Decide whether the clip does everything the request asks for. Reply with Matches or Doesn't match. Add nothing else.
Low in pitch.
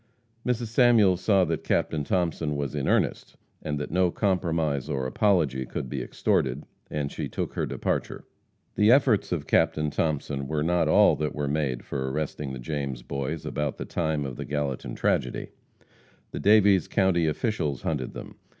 Matches